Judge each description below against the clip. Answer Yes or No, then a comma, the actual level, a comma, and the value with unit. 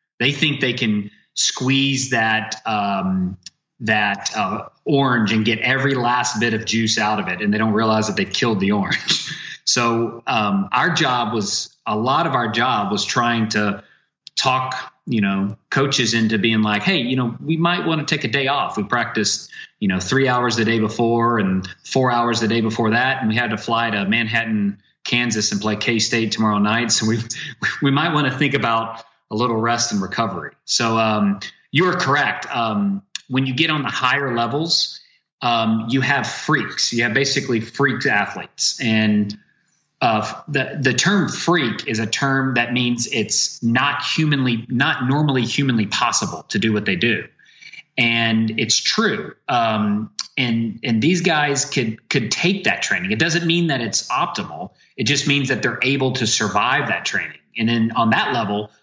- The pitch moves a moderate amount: Yes, average, 3.5 semitones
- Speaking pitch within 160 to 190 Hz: No, low, 115 Hz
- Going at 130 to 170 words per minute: No, average, 185 wpm